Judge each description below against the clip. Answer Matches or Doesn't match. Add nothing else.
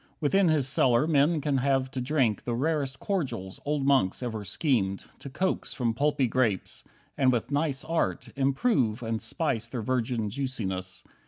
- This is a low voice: Matches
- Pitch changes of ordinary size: Matches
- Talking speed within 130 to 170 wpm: Matches